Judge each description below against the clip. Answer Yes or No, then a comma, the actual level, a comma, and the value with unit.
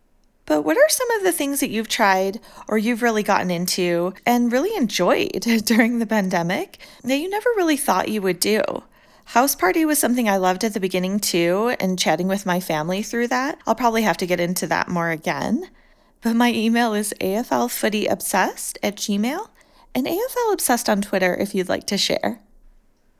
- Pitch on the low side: No, high, 220 Hz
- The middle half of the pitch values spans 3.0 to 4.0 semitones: No, average, 5.1 semitones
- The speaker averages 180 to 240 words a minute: Yes, average, 185 wpm